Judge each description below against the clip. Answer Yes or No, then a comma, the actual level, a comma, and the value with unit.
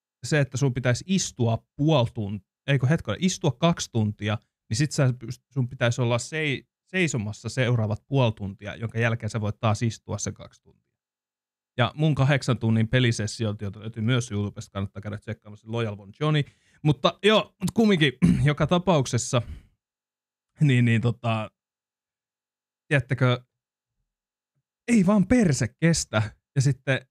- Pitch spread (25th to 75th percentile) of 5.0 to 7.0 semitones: Yes, average, 5.3 semitones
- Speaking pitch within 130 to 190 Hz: No, low, 120 Hz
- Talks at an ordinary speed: Yes, average, 135 wpm